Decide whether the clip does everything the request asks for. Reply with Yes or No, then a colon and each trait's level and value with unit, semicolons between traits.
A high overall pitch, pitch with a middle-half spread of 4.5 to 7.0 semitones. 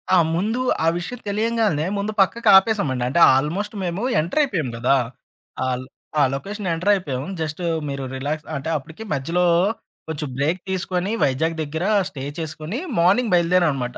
No: medium, 170 Hz; wide, 5.5 semitones